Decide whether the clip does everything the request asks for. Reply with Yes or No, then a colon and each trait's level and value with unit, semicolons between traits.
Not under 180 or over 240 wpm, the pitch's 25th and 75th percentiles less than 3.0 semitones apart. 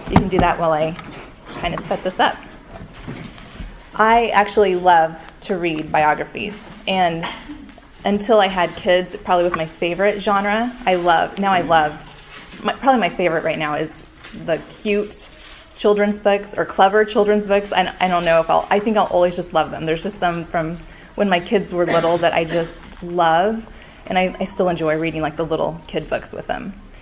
No: average, 195 wpm; average, 3.7 semitones